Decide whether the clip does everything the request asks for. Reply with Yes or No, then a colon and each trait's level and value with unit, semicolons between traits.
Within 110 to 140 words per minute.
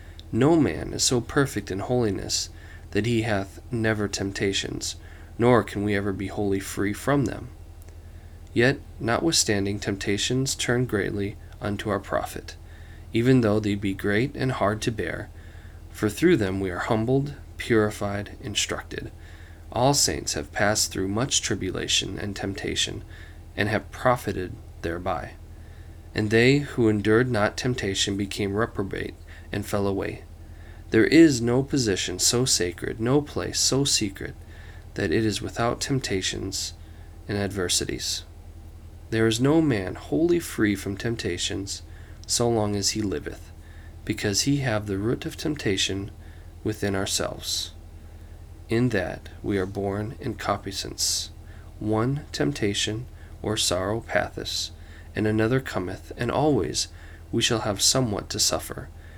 Yes: slow, 135 wpm